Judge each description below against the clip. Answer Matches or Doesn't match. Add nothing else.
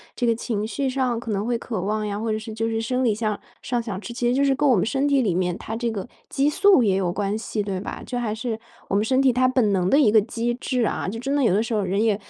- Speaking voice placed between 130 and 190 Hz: Doesn't match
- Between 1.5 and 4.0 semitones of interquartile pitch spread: Matches